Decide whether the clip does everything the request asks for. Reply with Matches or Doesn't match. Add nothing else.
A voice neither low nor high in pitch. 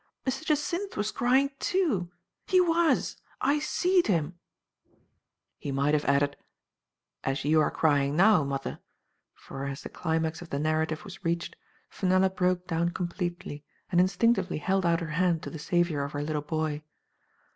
Matches